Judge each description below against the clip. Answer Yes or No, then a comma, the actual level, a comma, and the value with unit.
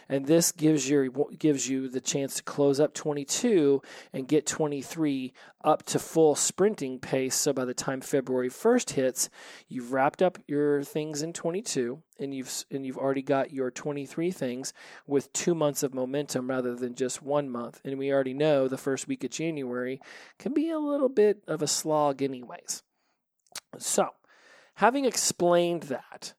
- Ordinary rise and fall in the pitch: Yes, average, 3.3 semitones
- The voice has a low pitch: No, medium, 145 Hz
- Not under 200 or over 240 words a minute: No, average, 170 wpm